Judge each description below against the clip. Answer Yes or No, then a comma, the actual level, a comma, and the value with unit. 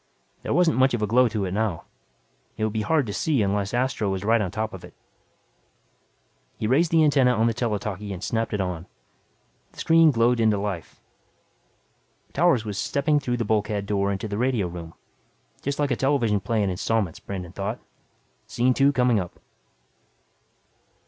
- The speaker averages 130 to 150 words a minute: No, average, 180 wpm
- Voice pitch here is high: No, low, 110 Hz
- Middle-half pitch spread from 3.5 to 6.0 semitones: Yes, average, 4.1 semitones